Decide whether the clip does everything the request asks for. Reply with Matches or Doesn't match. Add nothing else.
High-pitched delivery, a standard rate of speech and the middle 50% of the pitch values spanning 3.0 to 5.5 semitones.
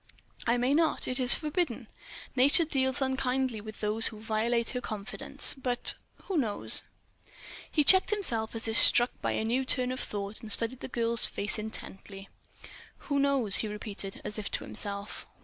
Matches